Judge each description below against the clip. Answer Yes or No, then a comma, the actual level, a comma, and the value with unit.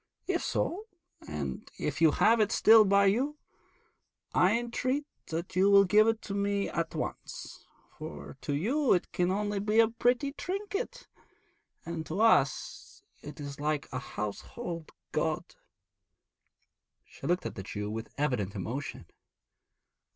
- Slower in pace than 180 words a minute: Yes, average, 145 wpm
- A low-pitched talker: No, high, 195 Hz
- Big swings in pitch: Yes, wide, 7.8 semitones